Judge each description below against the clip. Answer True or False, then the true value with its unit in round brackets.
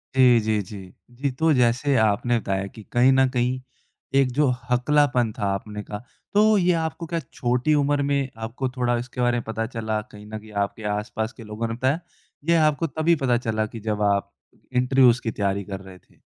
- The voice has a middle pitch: False (120 Hz)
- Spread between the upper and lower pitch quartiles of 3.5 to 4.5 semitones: True (3.8 semitones)